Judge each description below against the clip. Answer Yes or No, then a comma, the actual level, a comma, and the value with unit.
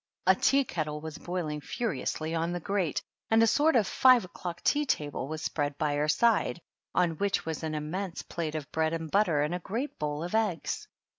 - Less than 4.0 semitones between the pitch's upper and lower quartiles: No, average, 4.8 semitones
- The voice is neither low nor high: Yes, medium, 165 Hz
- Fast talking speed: Yes, fast, 215 wpm